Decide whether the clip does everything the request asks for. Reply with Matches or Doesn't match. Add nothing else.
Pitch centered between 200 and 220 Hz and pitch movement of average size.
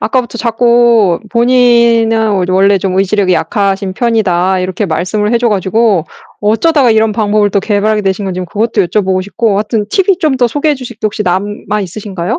Matches